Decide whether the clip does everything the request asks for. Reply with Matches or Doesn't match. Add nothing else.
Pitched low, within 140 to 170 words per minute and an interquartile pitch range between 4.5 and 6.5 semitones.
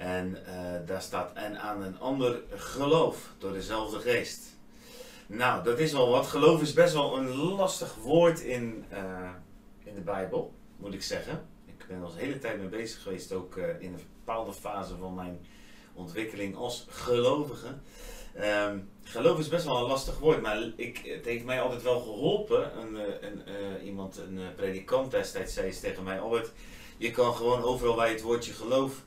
Doesn't match